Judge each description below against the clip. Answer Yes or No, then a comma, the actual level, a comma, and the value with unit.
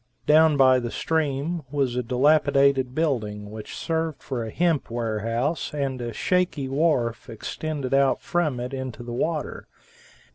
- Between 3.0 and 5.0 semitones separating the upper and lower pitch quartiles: Yes, average, 4.3 semitones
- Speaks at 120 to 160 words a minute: Yes, average, 145 wpm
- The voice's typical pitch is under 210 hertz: Yes, low, 135 Hz